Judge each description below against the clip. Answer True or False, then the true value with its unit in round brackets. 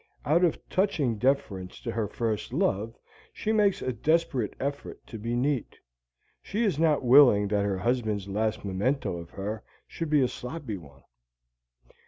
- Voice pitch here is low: True (120 Hz)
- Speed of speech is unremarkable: True (160 wpm)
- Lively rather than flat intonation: True (6.2 semitones)